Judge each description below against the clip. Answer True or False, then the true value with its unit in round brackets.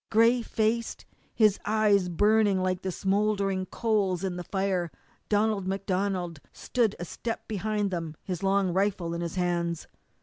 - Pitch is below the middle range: False (195 Hz)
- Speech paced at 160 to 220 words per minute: False (145 wpm)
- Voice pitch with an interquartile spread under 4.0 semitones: True (2.9 semitones)